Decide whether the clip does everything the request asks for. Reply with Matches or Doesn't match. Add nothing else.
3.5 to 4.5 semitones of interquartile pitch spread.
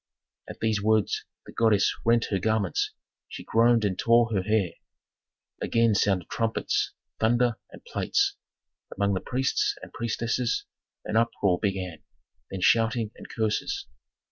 Doesn't match